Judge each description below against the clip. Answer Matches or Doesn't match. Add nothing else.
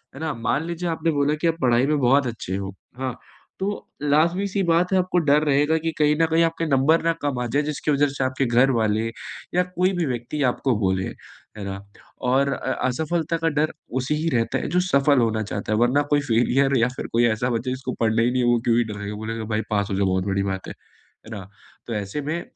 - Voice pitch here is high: Doesn't match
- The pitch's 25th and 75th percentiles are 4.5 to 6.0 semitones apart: Matches